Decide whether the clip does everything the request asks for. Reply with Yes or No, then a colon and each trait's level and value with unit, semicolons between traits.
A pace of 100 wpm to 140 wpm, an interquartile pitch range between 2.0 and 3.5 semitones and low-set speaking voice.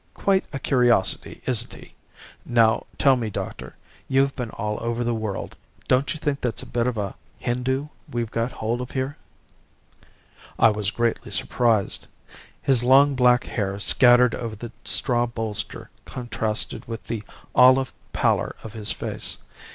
No: average, 150 wpm; narrow, 2.5 semitones; low, 120 Hz